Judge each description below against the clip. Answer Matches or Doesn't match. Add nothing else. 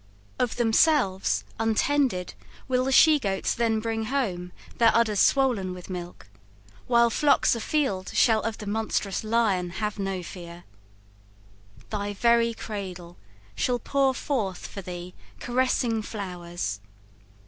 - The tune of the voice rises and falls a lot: Doesn't match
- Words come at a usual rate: Doesn't match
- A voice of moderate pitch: Doesn't match